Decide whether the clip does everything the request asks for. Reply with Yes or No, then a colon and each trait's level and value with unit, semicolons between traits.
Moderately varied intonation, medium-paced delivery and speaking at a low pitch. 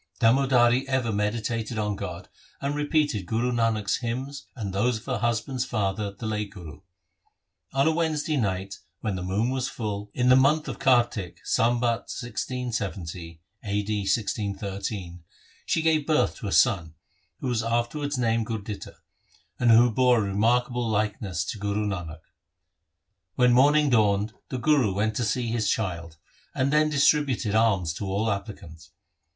Yes: average, 3.9 semitones; average, 155 wpm; low, 115 Hz